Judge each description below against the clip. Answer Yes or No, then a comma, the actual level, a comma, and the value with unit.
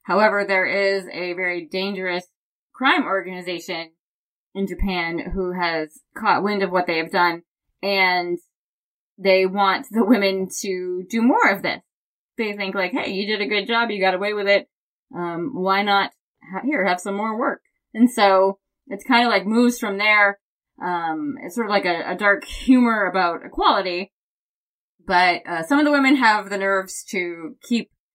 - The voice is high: Yes, high, 195 Hz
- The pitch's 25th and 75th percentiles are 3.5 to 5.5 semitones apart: No, average, 2.8 semitones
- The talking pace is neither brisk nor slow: Yes, average, 175 wpm